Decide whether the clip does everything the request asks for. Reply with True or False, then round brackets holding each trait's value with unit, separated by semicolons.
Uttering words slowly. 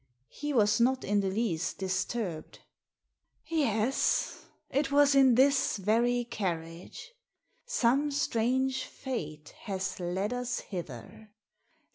True (105 wpm)